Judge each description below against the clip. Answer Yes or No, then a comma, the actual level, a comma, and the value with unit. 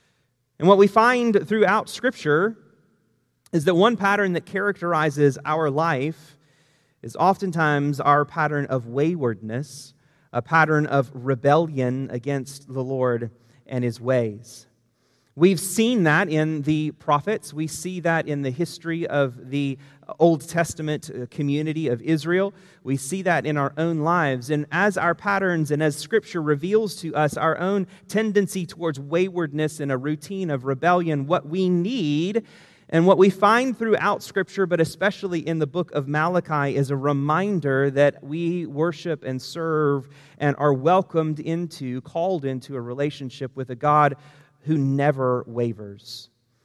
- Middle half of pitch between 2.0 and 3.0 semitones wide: No, average, 4.1 semitones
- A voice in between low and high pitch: Yes, medium, 155 Hz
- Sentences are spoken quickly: No, average, 145 wpm